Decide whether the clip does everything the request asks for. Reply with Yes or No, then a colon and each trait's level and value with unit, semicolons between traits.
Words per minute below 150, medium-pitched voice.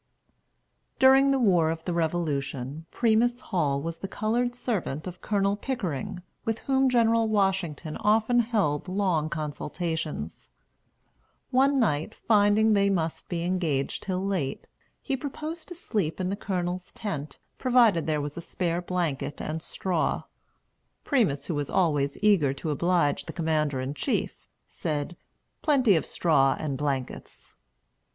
Yes: average, 140 wpm; medium, 180 Hz